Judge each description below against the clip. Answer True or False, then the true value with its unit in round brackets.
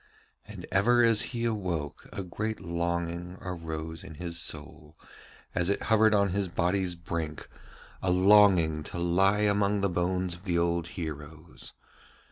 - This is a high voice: False (90 Hz)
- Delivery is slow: False (145 wpm)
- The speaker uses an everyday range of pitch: True (3.0 semitones)